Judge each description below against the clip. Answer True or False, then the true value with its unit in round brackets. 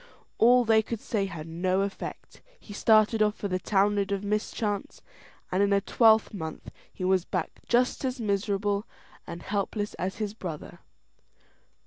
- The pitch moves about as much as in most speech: False (2.2 semitones)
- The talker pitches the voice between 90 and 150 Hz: False (200 Hz)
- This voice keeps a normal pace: True (150 wpm)